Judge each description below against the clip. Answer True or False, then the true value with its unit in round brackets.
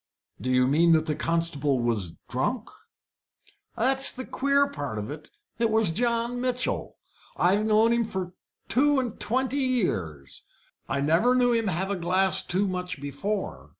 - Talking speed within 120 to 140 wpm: False (155 wpm)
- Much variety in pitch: True (8.1 semitones)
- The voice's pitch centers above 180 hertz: True (190 Hz)